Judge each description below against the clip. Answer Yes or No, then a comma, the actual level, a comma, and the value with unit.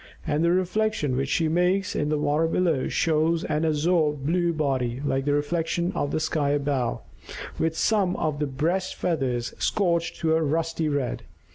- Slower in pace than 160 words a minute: No, average, 170 wpm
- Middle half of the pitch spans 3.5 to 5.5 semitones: No, average, 2.9 semitones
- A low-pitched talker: No, medium, 155 Hz